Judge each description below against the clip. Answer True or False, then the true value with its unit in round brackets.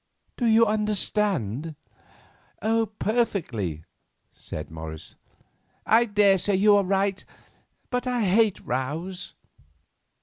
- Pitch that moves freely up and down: True (6.6 semitones)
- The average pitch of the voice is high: True (195 Hz)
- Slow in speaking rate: True (90 wpm)